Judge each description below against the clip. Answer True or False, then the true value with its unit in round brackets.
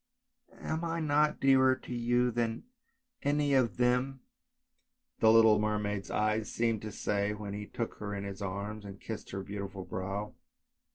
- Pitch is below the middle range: True (110 Hz)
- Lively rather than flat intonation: False (3.5 semitones)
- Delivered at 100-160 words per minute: False (170 wpm)